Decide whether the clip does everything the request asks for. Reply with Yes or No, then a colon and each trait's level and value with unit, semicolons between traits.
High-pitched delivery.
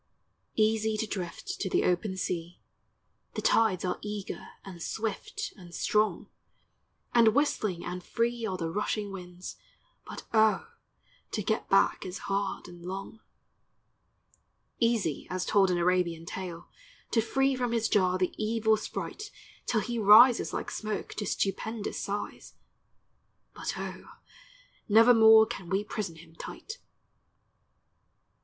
Yes: high, 205 Hz